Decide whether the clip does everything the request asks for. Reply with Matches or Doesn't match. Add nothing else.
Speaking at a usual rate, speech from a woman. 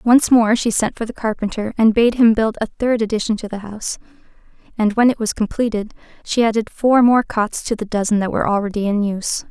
Doesn't match